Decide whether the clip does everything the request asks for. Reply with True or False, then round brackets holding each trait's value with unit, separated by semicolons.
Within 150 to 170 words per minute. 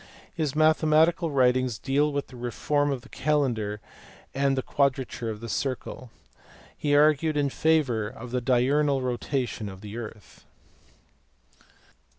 False (135 wpm)